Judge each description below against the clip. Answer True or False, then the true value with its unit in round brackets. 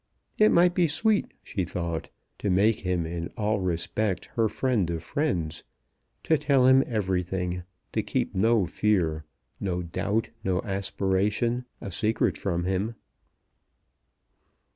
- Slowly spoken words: True (130 wpm)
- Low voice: True (100 Hz)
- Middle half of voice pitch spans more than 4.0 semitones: True (4.6 semitones)